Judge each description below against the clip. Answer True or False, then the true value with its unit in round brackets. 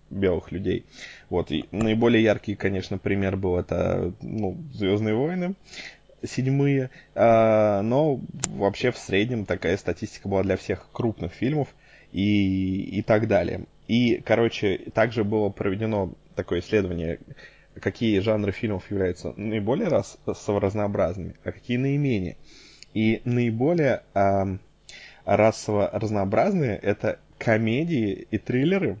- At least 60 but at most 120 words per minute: True (115 wpm)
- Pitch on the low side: True (105 Hz)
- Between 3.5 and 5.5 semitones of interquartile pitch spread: False (3.0 semitones)